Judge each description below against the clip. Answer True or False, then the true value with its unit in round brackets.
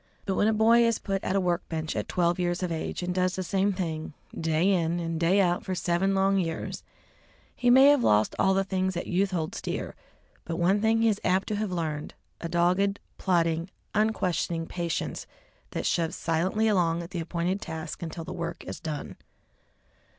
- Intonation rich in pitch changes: False (2.7 semitones)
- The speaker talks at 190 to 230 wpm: True (200 wpm)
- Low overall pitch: False (180 Hz)